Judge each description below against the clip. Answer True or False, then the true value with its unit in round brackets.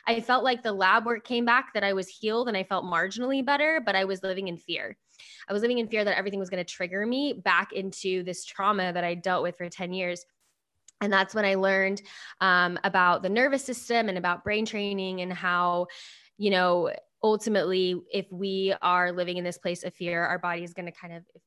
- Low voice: False (190 Hz)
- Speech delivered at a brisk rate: True (225 wpm)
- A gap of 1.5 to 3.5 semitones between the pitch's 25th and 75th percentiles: True (3.0 semitones)